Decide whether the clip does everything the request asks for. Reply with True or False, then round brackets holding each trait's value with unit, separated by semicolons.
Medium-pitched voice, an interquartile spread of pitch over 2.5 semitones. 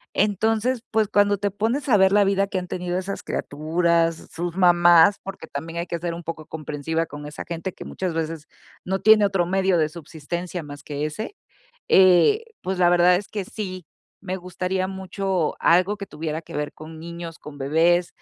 True (175 Hz; 2.9 semitones)